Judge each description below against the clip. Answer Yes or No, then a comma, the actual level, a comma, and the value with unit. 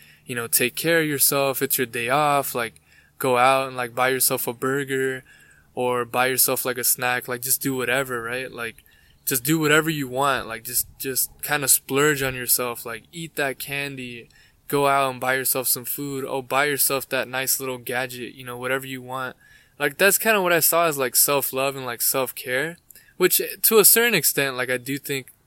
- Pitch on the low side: Yes, low, 130 Hz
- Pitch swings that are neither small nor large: No, narrow, 2.1 semitones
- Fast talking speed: Yes, fast, 210 wpm